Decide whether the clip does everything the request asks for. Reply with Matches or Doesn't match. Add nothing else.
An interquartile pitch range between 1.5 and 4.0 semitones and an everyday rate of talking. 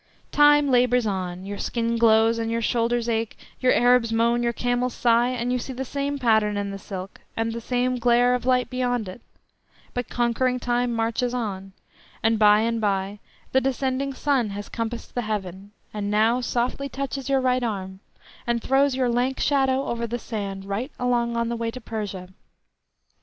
Matches